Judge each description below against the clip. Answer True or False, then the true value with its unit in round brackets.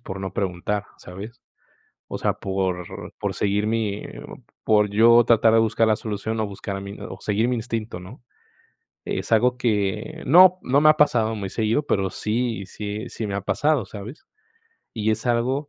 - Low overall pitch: True (110 Hz)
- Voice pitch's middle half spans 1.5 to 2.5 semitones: False (2.9 semitones)